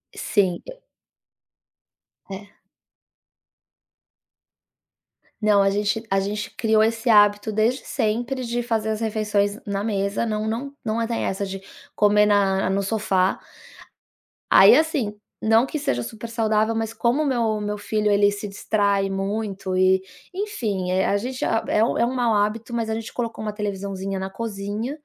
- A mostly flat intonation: Yes, narrow, 2.3 semitones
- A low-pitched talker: No, high, 210 Hz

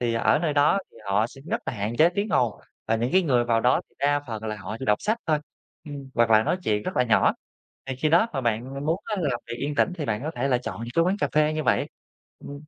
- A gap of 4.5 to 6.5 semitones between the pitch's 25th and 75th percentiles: Yes, average, 5.1 semitones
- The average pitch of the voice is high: No, low, 135 Hz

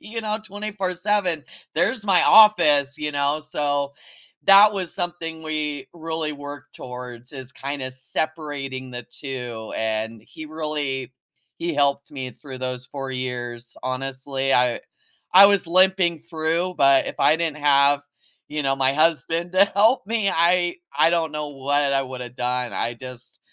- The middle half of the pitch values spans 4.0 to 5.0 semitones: Yes, average, 4.4 semitones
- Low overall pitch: No, medium, 145 Hz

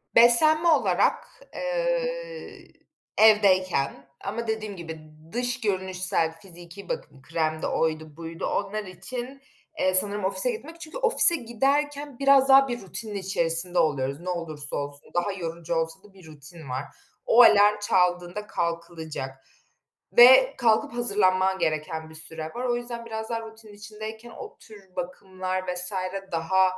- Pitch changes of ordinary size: No, wide, 6.1 semitones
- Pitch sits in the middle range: No, high, 195 Hz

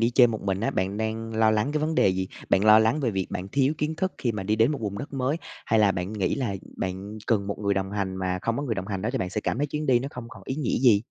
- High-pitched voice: No, low, 110 Hz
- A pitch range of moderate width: Yes, average, 4.6 semitones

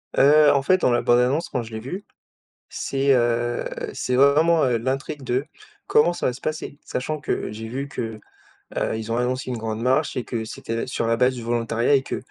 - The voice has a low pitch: Yes, low, 125 Hz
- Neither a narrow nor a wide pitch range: Yes, average, 3.2 semitones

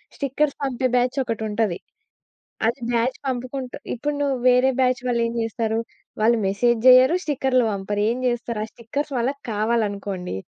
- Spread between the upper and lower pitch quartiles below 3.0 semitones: Yes, narrow, 2.6 semitones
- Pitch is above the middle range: Yes, high, 240 Hz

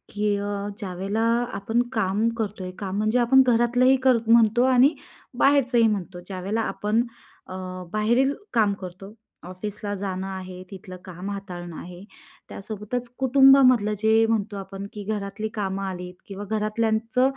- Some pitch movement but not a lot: Yes, average, 3.1 semitones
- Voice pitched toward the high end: Yes, high, 210 Hz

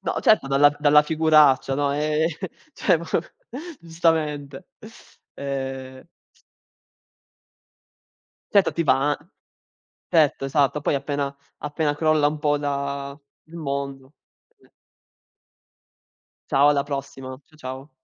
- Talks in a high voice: No, medium, 145 Hz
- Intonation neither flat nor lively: No, narrow, 1.8 semitones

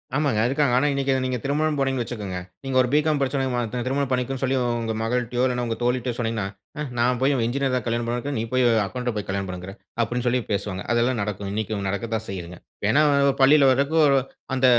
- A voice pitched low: Yes, low, 125 Hz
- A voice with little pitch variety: No, average, 3.1 semitones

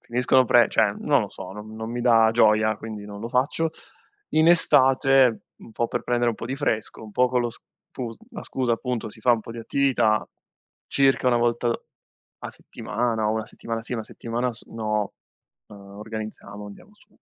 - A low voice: Yes, low, 115 Hz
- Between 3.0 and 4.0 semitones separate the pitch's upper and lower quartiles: No, narrow, 2.6 semitones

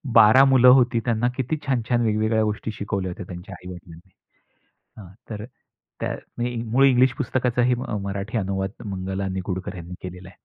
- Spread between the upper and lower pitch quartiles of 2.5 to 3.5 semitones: No, average, 4.3 semitones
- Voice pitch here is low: Yes, low, 105 Hz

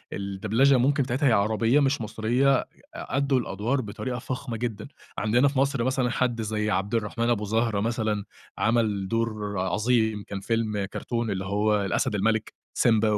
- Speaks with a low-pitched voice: Yes, low, 115 Hz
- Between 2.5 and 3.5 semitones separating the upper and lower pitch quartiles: Yes, average, 2.9 semitones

